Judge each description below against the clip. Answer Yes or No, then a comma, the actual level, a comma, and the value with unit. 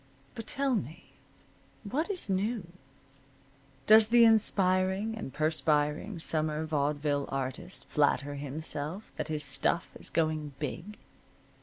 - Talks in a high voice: No, medium, 160 Hz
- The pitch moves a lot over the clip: Yes, wide, 6.2 semitones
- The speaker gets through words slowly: Yes, slow, 115 wpm